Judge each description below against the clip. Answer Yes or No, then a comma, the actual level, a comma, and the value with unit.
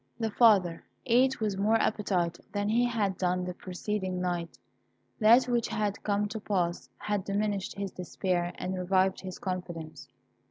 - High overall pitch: Yes, high, 195 Hz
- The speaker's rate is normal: Yes, average, 155 wpm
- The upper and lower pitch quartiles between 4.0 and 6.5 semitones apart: No, average, 2.9 semitones